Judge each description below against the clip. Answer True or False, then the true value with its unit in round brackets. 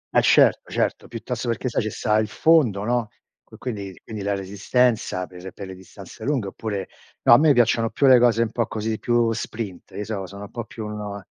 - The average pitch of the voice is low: True (110 Hz)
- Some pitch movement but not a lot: True (3.0 semitones)